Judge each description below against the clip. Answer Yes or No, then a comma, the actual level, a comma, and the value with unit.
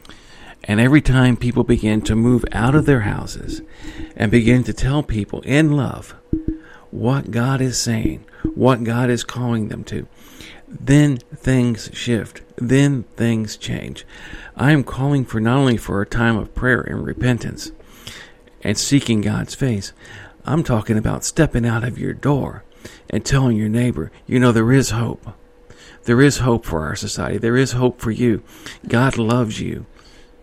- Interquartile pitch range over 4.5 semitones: No, average, 2.8 semitones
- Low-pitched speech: Yes, low, 120 Hz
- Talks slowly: No, average, 160 wpm